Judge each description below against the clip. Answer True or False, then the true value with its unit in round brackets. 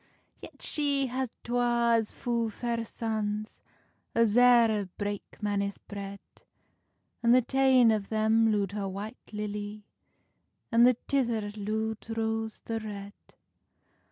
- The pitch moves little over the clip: True (2.3 semitones)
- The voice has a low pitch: False (220 Hz)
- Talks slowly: True (125 wpm)